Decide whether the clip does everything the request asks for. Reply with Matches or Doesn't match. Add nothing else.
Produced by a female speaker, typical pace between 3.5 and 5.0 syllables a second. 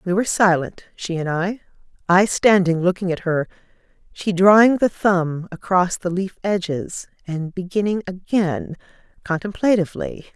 Matches